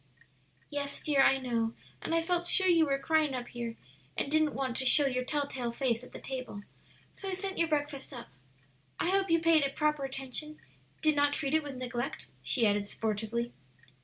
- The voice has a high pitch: Yes, very high, 275 Hz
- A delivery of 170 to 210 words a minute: Yes, average, 200 wpm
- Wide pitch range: No, average, 3.9 semitones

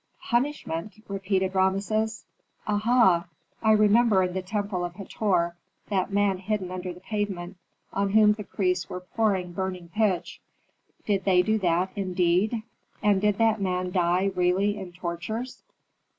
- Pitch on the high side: Yes, high, 195 Hz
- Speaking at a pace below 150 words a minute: Yes, average, 140 wpm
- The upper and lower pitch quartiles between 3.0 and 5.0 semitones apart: No, narrow, 2.6 semitones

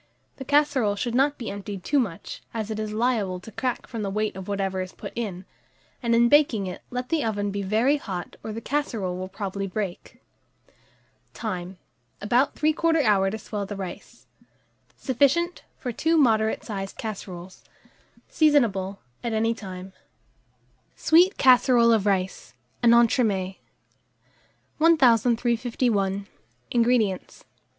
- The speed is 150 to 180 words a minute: No, average, 140 wpm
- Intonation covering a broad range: No, average, 4.3 semitones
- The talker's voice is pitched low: No, high, 220 Hz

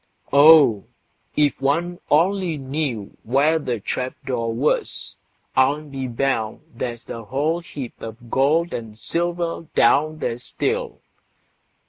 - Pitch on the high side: No, medium, 140 Hz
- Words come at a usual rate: No, slow, 120 wpm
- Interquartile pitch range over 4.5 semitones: Yes, average, 5.2 semitones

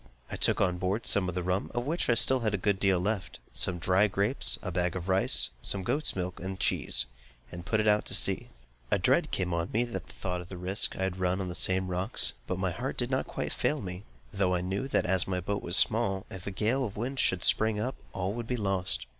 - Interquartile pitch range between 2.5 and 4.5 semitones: Yes, average, 3.1 semitones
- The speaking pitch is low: Yes, very low, 95 Hz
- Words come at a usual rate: No, fast, 250 wpm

